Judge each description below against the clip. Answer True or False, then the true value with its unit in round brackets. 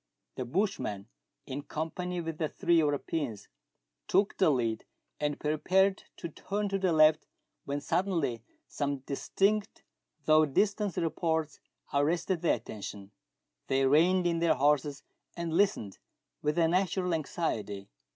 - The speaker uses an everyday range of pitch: True (4.2 semitones)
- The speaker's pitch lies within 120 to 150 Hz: False (160 Hz)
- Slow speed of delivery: True (130 wpm)